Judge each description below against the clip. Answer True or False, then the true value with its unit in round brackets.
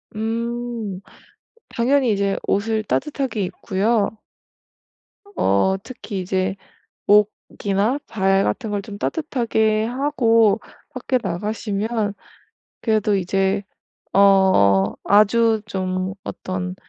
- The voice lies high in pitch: True (210 Hz)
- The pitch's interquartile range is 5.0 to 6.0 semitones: False (3.0 semitones)